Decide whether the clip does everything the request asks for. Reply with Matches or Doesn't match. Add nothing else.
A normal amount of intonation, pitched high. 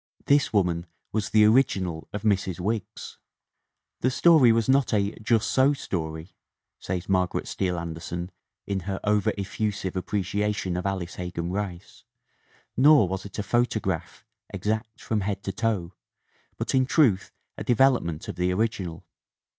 Doesn't match